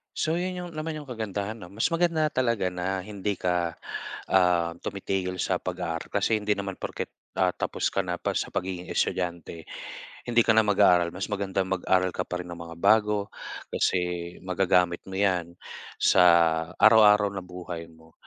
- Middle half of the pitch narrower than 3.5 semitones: Yes, average, 3.0 semitones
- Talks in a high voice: No, very low, 95 Hz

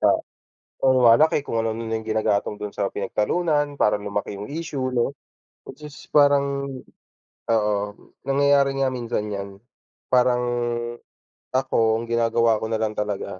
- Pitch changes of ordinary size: Yes, average, 4.6 semitones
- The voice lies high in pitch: No, low, 115 Hz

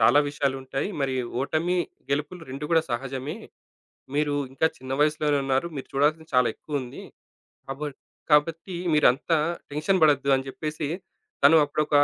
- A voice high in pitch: No, medium, 145 Hz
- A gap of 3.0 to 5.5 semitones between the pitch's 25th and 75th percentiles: No, narrow, 2.4 semitones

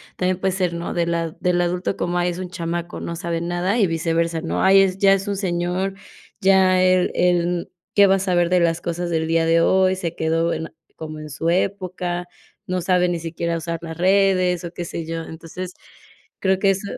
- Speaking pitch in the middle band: Yes, medium, 175 Hz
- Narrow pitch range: Yes, narrow, 1.8 semitones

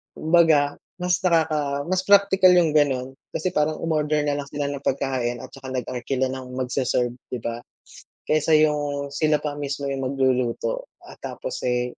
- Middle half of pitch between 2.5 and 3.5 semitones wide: Yes, average, 3.2 semitones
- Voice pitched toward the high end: No, medium, 145 Hz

